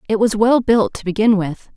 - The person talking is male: No, female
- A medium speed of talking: No, fast, 240 wpm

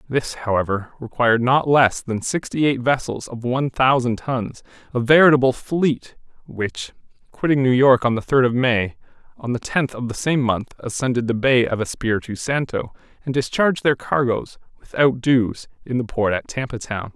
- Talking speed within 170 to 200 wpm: Yes, average, 175 wpm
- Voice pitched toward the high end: No, low, 125 Hz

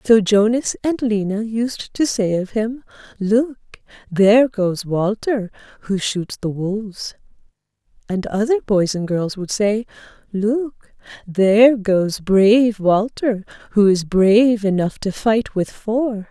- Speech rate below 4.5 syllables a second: Yes, 3.8 syllables/s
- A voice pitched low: No, high, 210 Hz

